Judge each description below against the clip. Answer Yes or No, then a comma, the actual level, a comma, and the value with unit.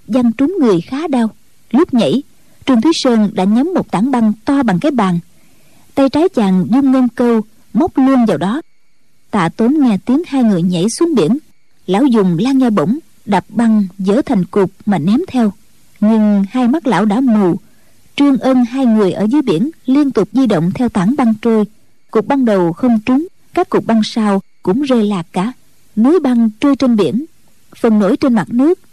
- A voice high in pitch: Yes, high, 235 Hz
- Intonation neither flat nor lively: Yes, average, 4.5 semitones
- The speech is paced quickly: No, average, 195 wpm